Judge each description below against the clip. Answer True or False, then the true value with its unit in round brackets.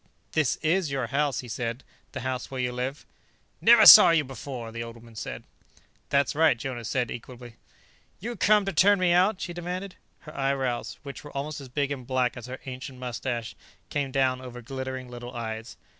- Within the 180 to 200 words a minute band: True (190 wpm)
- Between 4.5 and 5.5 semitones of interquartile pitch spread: False (3.4 semitones)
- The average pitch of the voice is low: True (130 Hz)